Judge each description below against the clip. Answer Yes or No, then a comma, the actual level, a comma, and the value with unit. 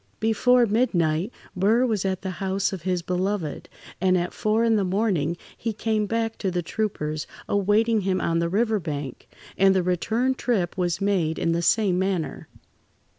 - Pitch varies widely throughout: No, average, 3.9 semitones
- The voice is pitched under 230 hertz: Yes, high, 190 Hz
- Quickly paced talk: No, average, 175 wpm